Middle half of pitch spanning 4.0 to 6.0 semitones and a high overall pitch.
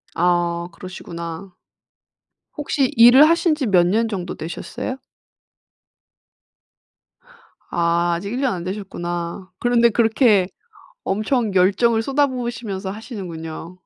Yes: wide, 5.5 semitones; high, 200 Hz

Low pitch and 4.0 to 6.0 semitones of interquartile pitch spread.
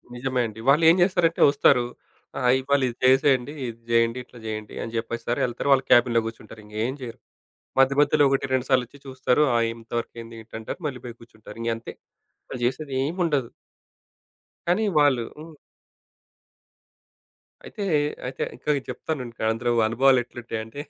No: low, 125 Hz; average, 3.1 semitones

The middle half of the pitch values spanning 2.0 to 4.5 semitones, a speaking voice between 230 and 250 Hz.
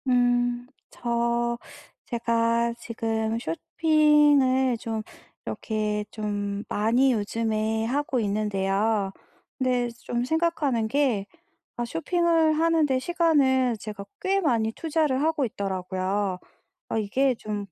Yes: average, 4.2 semitones; high, 235 Hz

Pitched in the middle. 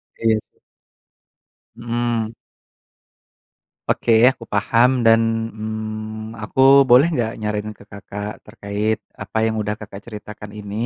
No: low, 110 Hz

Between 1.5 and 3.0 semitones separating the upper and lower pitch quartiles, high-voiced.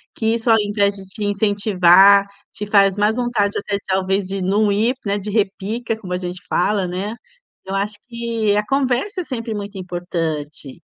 Yes: narrow, 2.5 semitones; high, 205 Hz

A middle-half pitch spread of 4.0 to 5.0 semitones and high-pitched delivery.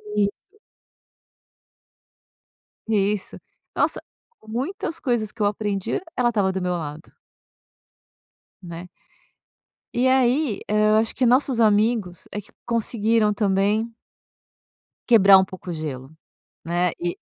No: average, 3.6 semitones; high, 210 Hz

